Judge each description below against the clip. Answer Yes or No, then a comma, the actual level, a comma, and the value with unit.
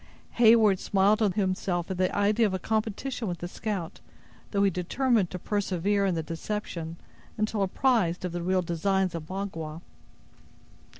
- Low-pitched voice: No, high, 190 Hz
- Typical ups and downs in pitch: Yes, average, 3.2 semitones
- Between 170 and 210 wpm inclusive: No, average, 160 wpm